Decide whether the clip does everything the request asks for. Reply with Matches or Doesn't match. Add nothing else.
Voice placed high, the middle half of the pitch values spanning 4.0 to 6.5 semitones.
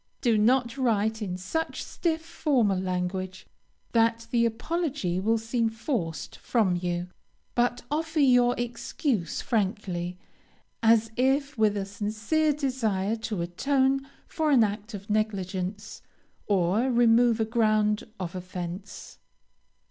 Matches